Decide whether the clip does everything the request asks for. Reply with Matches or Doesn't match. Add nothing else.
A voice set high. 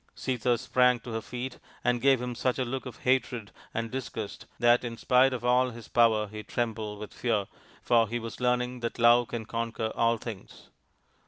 Doesn't match